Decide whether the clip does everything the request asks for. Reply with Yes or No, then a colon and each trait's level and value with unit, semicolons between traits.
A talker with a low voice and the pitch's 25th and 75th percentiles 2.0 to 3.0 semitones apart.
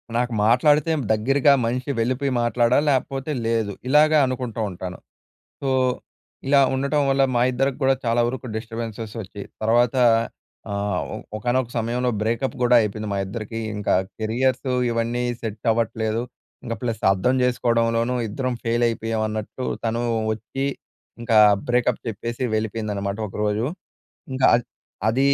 Yes: low, 115 Hz; average, 2.7 semitones